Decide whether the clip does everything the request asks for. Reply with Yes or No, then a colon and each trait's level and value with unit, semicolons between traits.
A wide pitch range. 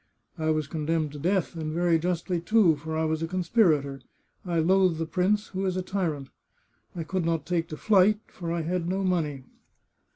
No: narrow, 2.6 semitones